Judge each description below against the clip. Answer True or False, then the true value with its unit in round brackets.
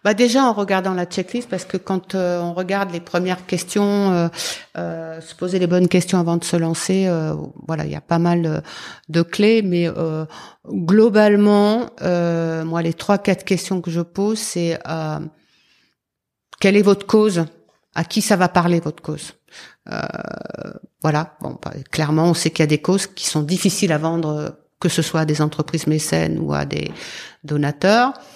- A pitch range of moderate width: True (3.2 semitones)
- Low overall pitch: False (175 Hz)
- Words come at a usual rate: True (190 wpm)